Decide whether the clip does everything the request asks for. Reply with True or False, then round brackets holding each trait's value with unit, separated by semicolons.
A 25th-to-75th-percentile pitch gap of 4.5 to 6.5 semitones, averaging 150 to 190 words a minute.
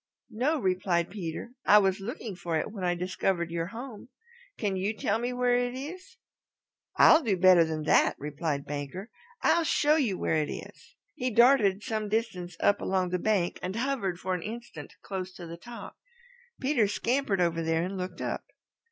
True (5.2 semitones; 180 wpm)